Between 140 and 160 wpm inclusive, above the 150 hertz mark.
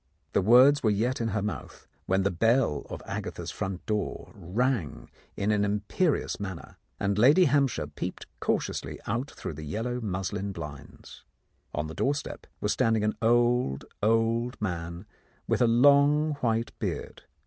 No: average, 155 wpm; low, 110 Hz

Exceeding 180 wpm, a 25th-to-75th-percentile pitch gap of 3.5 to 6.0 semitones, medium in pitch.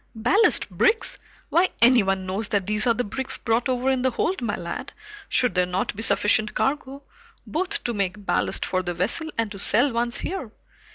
No: average, 190 wpm; average, 4.7 semitones; high, 230 Hz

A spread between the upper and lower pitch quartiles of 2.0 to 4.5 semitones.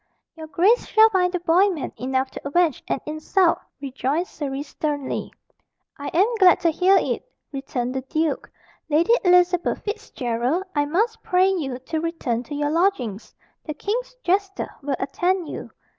No: average, 4.9 semitones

